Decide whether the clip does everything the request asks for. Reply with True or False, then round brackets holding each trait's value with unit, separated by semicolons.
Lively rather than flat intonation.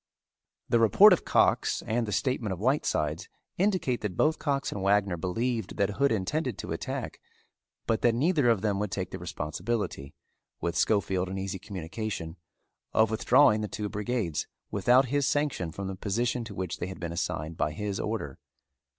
False (4.6 semitones)